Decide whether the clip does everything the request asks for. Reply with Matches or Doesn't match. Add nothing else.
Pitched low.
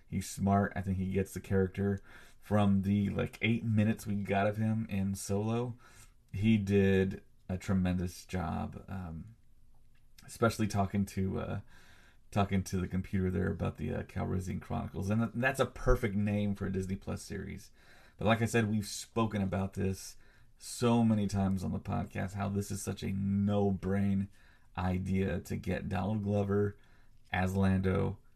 Matches